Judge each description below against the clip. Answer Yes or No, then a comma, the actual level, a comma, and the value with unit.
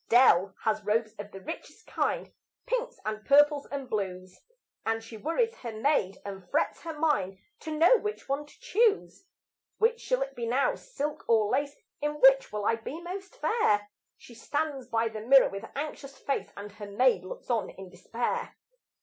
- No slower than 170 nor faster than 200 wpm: Yes, average, 180 wpm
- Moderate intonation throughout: No, wide, 6.3 semitones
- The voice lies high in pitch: Yes, very high, 255 Hz